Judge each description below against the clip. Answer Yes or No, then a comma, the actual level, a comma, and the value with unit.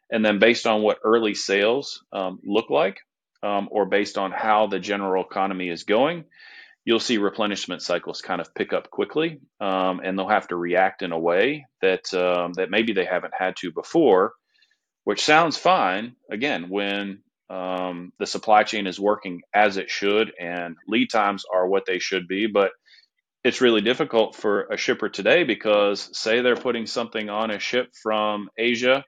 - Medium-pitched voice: No, low, 100 Hz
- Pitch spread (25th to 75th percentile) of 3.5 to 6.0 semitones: No, average, 3.0 semitones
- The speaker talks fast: No, average, 180 wpm